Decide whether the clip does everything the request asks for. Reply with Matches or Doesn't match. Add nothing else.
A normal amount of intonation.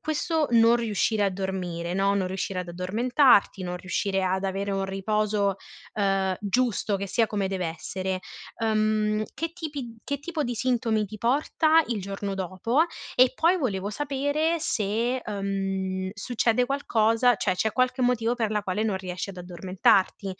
Matches